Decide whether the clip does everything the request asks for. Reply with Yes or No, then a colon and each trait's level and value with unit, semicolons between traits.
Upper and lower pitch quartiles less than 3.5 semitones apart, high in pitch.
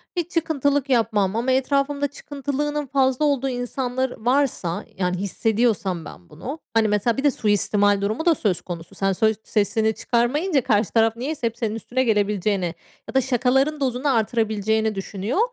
No: average, 4.7 semitones; high, 235 Hz